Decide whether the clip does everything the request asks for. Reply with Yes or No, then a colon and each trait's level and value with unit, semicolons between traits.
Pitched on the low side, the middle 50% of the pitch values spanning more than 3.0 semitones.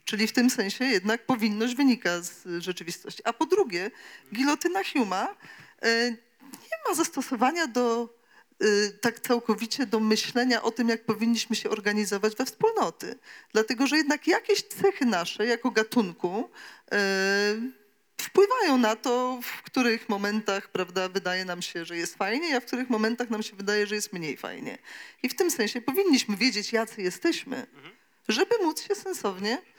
No: high, 230 Hz; average, 4.1 semitones